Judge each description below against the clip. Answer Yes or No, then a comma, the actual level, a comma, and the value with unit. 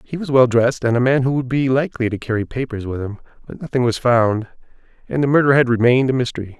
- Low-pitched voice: Yes, low, 125 Hz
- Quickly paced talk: Yes, fast, 245 wpm